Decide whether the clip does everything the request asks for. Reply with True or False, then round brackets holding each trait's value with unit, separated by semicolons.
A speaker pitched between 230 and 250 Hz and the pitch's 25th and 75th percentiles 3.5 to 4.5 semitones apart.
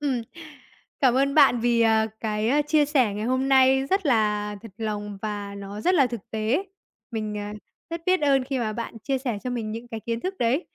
True (235 Hz; 4.0 semitones)